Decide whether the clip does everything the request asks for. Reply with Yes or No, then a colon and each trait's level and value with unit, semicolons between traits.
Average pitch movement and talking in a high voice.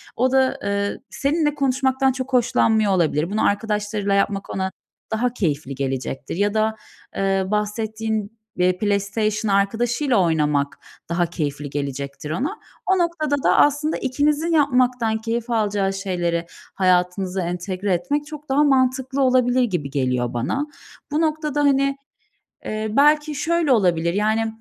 No: wide, 6.5 semitones; high, 220 Hz